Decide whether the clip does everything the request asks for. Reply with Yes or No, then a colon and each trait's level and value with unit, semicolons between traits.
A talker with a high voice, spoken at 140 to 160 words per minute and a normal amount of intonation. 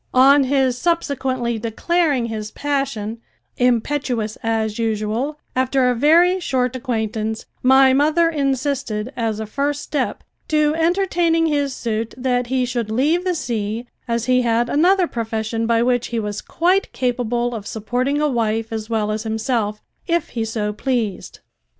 Yes: high, 245 Hz; average, 150 wpm; average, 4.3 semitones